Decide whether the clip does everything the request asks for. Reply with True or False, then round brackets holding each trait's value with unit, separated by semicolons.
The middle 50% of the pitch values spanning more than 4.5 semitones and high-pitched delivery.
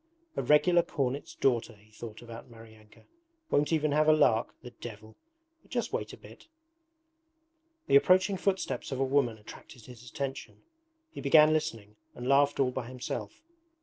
False (4.9 semitones; 130 Hz)